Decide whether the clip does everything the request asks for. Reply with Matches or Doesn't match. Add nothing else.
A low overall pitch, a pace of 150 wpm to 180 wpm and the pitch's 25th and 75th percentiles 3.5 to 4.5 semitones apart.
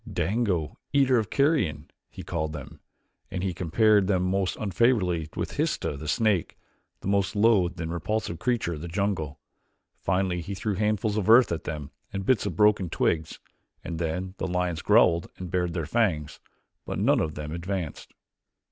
Matches